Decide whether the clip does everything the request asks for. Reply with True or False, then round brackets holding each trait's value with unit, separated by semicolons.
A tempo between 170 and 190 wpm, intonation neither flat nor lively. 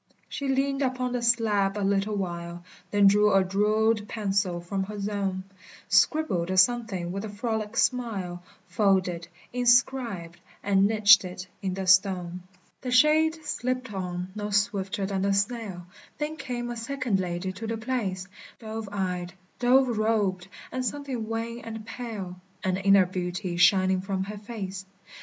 False (150 wpm; 3.8 semitones)